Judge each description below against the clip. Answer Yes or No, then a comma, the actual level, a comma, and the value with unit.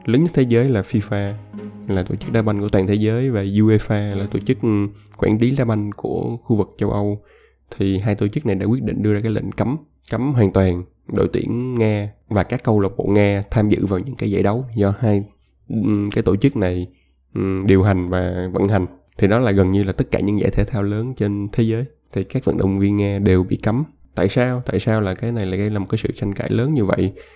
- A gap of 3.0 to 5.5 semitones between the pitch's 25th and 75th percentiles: No, narrow, 2.5 semitones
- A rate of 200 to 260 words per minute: Yes, fast, 250 wpm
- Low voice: Yes, low, 105 Hz